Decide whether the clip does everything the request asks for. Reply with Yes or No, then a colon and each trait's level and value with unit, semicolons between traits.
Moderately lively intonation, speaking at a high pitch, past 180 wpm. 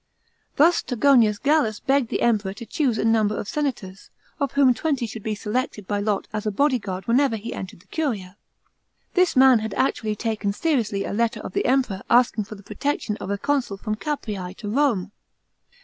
Yes: average, 4.7 semitones; high, 225 Hz; average, 190 wpm